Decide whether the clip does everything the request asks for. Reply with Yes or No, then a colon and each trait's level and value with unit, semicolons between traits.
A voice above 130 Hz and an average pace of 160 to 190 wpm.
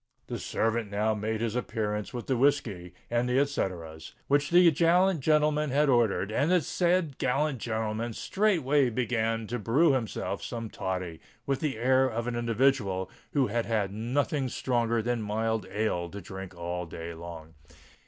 No: low, 115 Hz; average, 165 wpm